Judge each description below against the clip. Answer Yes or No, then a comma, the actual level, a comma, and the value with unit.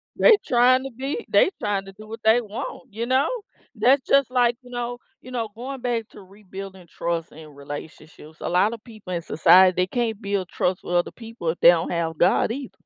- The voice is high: Yes, high, 215 Hz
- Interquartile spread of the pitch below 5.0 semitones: No, average, 5.3 semitones